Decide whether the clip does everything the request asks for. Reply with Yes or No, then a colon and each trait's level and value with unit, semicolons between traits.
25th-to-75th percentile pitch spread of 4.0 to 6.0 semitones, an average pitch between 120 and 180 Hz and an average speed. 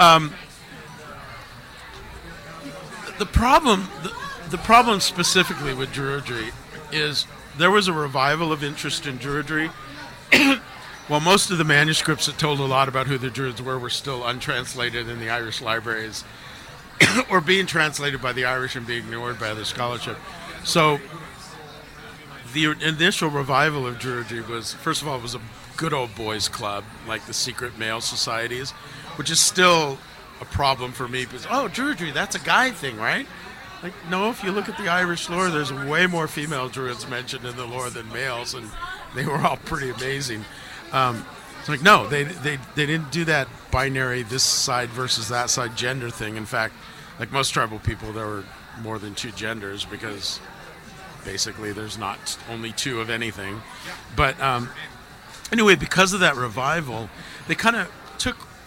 Yes: average, 4.9 semitones; low, 135 Hz; average, 170 wpm